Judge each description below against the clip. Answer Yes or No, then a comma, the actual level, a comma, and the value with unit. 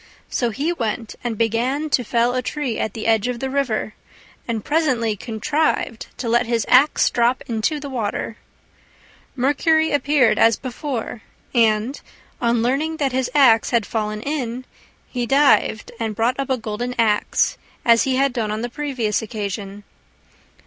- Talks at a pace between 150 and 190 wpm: Yes, average, 160 wpm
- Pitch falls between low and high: No, high, 240 Hz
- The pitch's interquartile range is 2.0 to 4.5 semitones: Yes, average, 3.4 semitones